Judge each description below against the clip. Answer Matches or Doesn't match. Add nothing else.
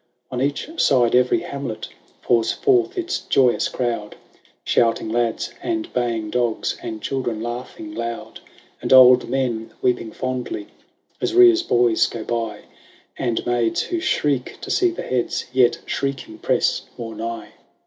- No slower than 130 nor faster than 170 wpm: Matches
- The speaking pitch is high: Doesn't match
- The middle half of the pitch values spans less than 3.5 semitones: Matches